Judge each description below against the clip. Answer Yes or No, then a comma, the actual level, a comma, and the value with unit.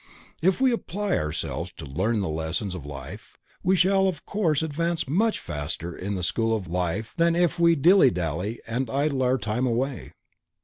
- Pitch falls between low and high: No, low, 125 Hz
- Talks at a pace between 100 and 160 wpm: No, average, 180 wpm